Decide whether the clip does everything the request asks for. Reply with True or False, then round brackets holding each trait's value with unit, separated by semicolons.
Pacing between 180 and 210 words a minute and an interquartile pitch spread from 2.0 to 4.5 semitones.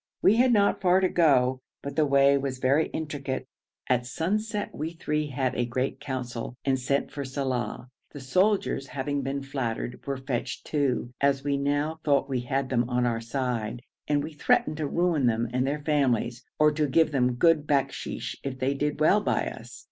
True (190 wpm; 2.9 semitones)